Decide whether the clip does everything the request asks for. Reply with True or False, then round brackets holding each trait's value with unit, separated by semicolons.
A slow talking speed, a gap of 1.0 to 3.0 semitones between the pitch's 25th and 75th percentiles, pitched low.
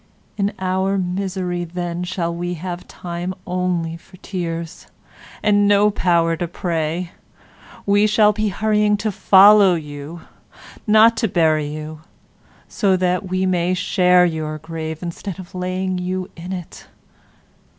False (130 wpm; 2.5 semitones; 180 Hz)